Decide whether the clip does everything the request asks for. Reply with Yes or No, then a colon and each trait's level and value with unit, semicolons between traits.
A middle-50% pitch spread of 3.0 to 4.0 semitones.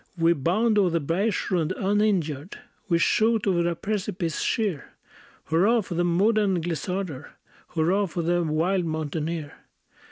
Yes: average, 3.6 semitones